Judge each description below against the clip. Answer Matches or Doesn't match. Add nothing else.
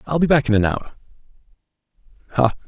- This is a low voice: Matches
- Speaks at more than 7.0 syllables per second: Matches